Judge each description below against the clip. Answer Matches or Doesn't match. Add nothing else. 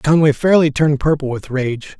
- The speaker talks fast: Doesn't match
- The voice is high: Doesn't match